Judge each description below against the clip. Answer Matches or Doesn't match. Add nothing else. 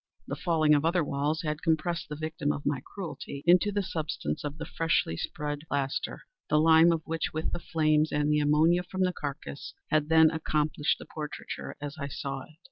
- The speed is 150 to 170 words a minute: Doesn't match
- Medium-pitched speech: Matches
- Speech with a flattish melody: Matches